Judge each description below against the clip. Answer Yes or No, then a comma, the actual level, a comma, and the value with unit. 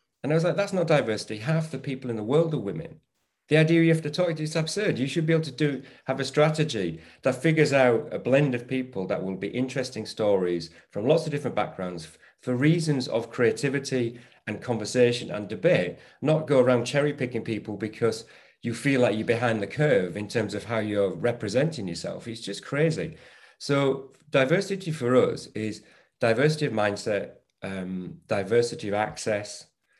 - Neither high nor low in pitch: No, low, 125 Hz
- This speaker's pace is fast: No, average, 190 wpm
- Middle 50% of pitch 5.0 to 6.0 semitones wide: Yes, wide, 5.6 semitones